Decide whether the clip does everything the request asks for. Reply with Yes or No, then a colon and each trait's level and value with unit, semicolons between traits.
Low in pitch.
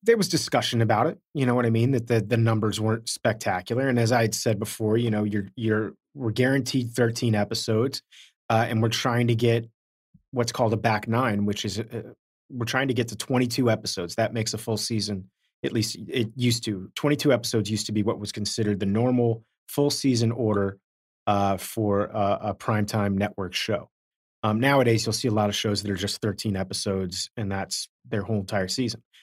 Yes: low, 115 Hz